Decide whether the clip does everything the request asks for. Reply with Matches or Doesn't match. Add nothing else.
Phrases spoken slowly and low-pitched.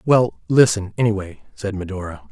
Matches